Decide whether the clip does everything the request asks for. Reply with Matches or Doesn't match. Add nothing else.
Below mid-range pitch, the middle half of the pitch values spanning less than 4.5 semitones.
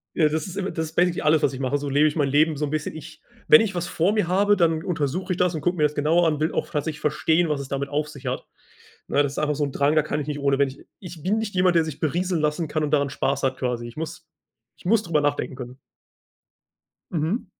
Doesn't match